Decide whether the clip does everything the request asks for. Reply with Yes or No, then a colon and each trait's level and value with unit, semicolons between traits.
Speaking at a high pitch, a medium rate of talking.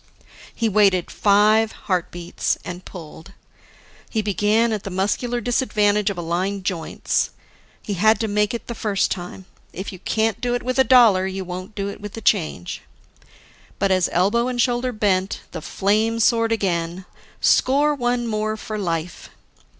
Yes: high, 205 Hz; average, 160 wpm